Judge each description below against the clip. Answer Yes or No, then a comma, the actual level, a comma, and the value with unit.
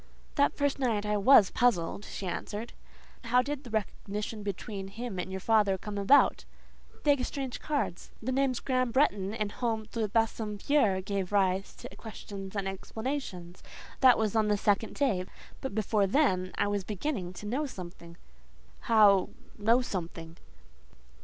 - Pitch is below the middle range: No, high, 210 Hz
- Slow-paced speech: No, average, 150 wpm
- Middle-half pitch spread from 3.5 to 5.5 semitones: Yes, average, 4.2 semitones